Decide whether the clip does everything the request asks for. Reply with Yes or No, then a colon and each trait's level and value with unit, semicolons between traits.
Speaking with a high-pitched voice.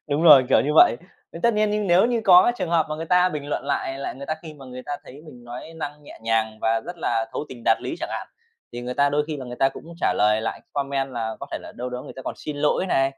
No: medium, 140 Hz